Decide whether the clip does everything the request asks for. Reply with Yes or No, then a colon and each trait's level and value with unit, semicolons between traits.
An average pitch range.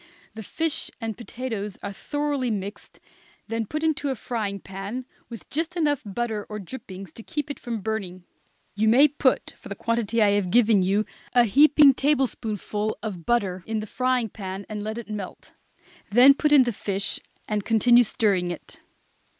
Yes: average, 4.2 semitones